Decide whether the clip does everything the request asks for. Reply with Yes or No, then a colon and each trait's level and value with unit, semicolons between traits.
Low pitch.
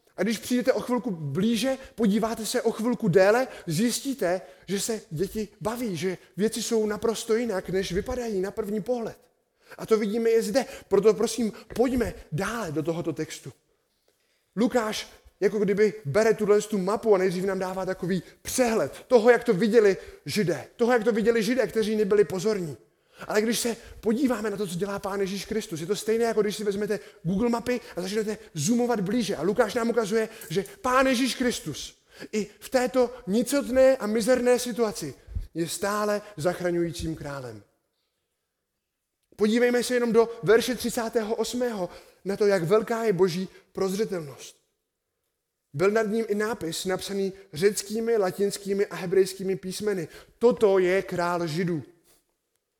No: high, 215 Hz